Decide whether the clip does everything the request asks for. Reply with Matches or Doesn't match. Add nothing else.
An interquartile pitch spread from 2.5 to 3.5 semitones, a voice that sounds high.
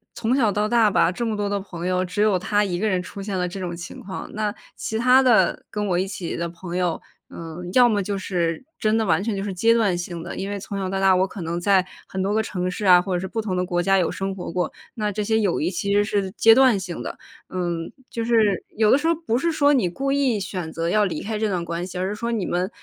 Matches